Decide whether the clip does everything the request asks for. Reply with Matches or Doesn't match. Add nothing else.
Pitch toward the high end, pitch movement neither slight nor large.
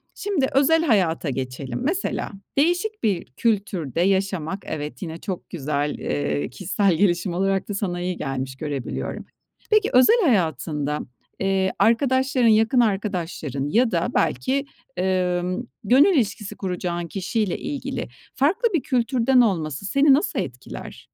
Doesn't match